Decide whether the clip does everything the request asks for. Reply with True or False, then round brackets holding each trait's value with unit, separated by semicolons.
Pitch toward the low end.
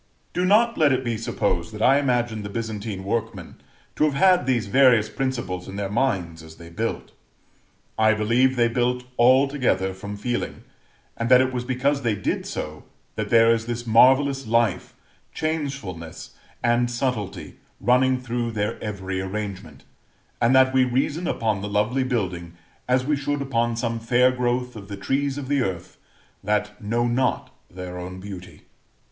True (115 Hz)